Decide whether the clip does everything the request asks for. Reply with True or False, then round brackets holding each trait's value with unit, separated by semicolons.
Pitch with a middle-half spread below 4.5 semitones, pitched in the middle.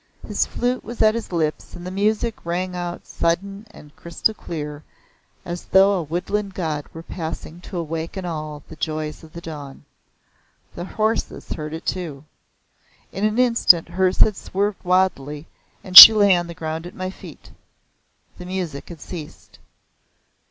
True (3.5 semitones; 175 Hz)